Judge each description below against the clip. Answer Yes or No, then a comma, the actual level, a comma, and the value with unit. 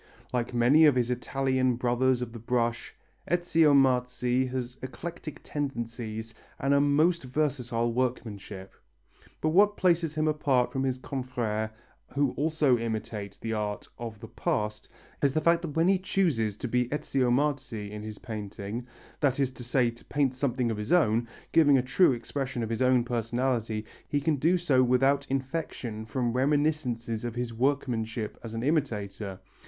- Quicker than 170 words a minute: No, average, 165 wpm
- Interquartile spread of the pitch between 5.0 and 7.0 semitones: No, average, 3.7 semitones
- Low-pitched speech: Yes, low, 125 Hz